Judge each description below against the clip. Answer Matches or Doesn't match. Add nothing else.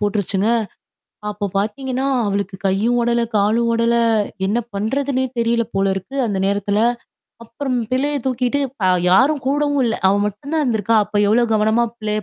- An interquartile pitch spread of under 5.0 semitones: Matches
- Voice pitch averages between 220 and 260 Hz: Matches